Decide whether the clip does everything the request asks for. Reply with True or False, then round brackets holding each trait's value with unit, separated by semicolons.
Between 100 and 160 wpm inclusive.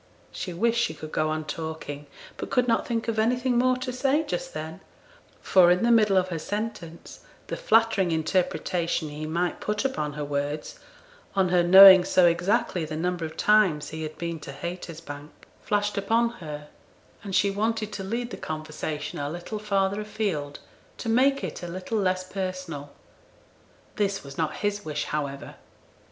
False (170 wpm)